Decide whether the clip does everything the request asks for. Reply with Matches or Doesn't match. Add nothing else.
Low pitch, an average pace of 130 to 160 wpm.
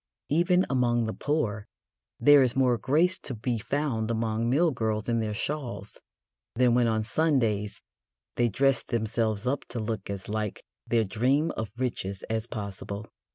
Matches